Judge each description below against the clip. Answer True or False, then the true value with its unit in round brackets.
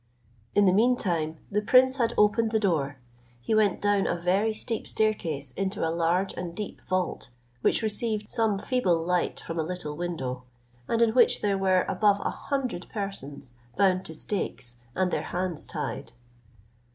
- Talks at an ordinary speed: True (170 wpm)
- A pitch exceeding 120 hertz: True (190 Hz)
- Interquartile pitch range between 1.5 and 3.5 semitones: False (4.2 semitones)